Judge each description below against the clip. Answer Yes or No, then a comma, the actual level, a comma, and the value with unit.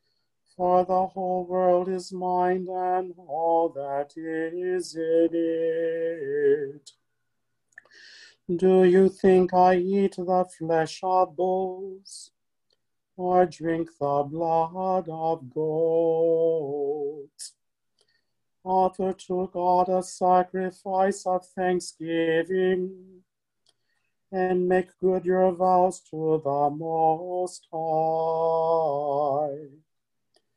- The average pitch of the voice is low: No, medium, 180 Hz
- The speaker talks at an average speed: No, slow, 85 wpm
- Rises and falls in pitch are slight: Yes, narrow, 2.1 semitones